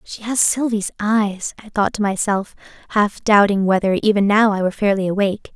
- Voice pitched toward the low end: No, high, 205 Hz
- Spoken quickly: No, average, 185 wpm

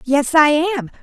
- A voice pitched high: Yes, very high, 295 Hz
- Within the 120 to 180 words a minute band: Yes, average, 175 wpm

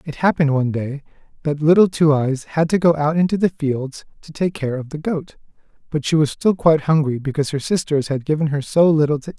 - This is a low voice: No, medium, 150 Hz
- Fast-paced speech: Yes, fast, 235 wpm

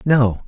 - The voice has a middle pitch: No, low, 115 Hz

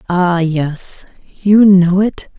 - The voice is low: No, medium, 185 Hz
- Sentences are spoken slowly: Yes, slow, 125 wpm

